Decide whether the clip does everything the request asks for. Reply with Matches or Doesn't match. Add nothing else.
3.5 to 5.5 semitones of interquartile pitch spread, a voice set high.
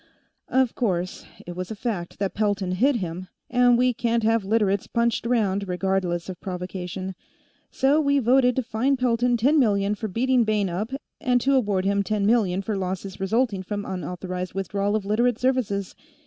Matches